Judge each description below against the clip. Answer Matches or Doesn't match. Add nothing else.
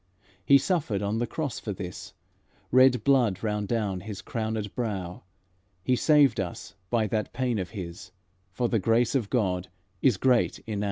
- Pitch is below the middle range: Matches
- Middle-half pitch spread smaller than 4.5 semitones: Matches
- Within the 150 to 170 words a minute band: Matches